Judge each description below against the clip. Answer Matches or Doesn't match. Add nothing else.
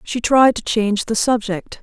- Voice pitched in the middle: Doesn't match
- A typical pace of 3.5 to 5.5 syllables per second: Matches